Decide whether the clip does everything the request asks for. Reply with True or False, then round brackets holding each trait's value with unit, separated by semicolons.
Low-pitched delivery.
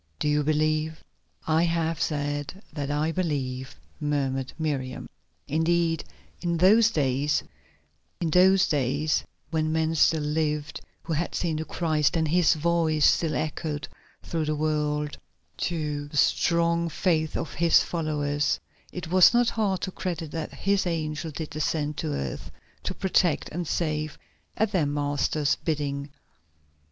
False (155 Hz)